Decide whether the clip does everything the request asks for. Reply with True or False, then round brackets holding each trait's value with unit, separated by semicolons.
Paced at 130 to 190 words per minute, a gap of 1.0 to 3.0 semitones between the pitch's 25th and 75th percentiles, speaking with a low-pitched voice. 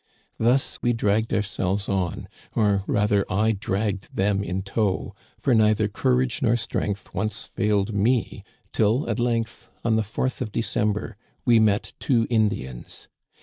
True (150 wpm; 2.4 semitones; 105 Hz)